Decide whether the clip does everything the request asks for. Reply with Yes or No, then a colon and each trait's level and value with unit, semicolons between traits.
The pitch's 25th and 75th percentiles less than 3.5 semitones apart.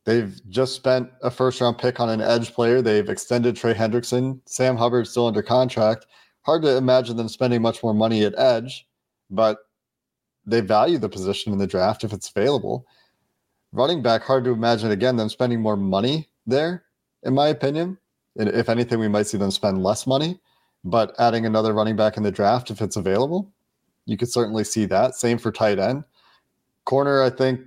Yes: average, 2.8 semitones